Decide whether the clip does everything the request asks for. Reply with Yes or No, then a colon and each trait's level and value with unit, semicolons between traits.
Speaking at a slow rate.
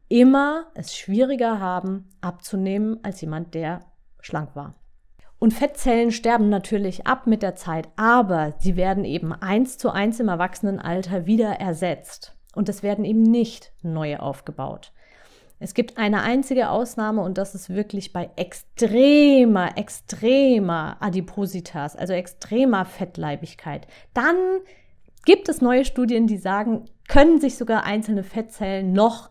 No: average, 135 wpm